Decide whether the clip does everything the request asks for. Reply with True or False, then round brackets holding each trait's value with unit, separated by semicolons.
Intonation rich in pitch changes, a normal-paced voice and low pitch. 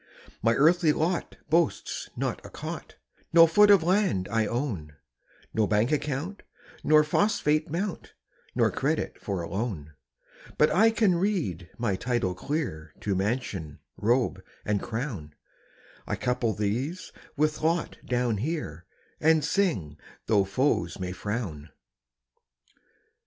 False (8.8 semitones; 125 wpm; 125 Hz)